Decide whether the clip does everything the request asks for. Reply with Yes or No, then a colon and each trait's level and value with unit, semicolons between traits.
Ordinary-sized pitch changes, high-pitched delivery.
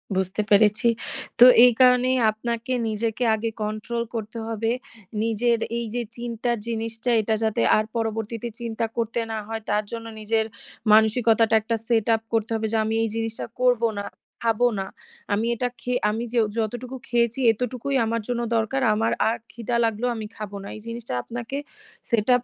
No: narrow, 1.5 semitones; high, 230 Hz